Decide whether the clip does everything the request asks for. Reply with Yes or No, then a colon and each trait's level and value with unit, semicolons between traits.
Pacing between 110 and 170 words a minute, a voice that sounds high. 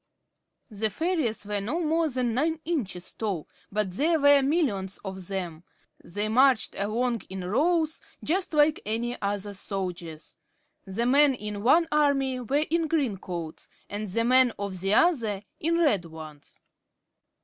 Yes: average, 150 wpm; high, 230 Hz